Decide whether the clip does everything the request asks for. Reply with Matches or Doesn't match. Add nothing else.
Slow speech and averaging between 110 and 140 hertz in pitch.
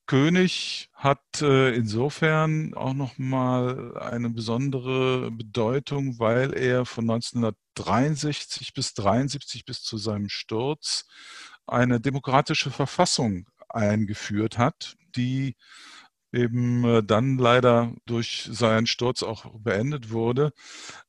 Matches